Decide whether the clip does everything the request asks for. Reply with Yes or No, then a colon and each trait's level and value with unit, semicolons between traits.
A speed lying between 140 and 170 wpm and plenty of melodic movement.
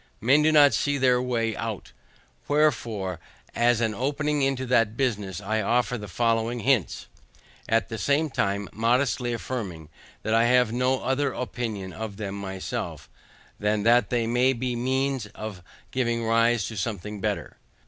No: average, 160 wpm; average, 3.2 semitones